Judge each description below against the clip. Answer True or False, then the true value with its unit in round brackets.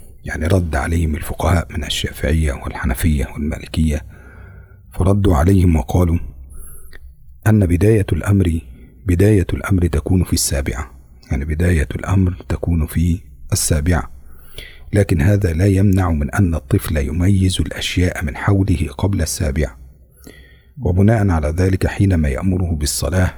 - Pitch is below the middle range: True (85 Hz)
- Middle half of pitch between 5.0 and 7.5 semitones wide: False (4.1 semitones)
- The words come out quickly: False (115 wpm)